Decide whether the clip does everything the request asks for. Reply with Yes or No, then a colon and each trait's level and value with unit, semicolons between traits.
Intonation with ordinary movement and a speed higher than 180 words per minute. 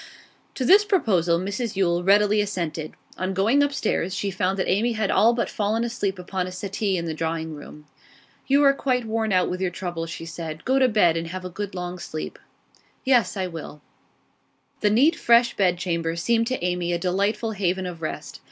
Yes: average, 4.4 semitones; average, 195 wpm